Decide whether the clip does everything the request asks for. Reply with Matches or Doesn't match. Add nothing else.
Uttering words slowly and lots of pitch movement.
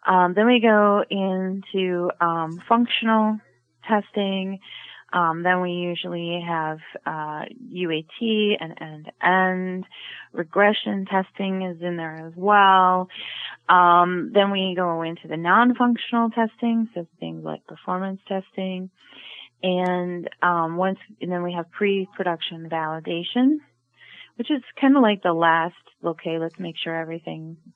Doesn't match